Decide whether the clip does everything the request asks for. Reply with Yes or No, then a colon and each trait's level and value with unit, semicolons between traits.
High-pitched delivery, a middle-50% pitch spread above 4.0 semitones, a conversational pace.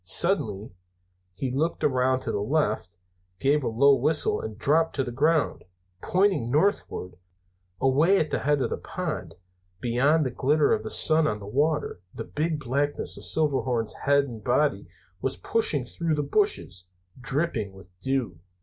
No: low, 135 Hz; average, 4.8 semitones; average, 160 wpm